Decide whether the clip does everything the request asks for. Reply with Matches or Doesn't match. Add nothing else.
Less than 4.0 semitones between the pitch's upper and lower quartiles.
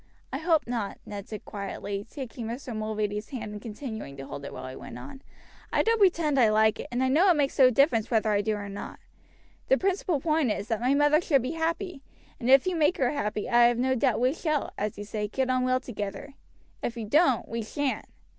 Doesn't match